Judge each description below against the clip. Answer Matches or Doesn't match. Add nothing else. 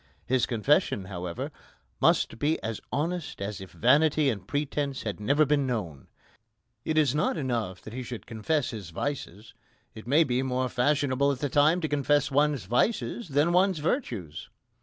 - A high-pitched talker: Doesn't match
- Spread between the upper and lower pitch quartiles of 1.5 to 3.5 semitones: Doesn't match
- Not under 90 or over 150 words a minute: Doesn't match